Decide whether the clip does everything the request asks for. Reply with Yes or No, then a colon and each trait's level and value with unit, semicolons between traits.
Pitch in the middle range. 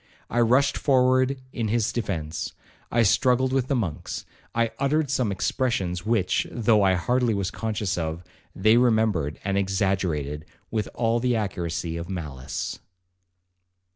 No: low, 110 Hz